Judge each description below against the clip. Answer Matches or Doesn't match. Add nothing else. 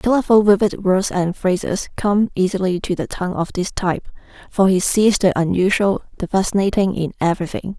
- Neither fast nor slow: Matches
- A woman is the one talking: Matches